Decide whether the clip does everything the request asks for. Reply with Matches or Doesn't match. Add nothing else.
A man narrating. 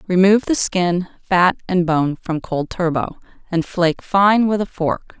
Doesn't match